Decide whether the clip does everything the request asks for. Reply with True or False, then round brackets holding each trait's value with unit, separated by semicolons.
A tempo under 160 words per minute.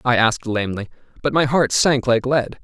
False (205 wpm)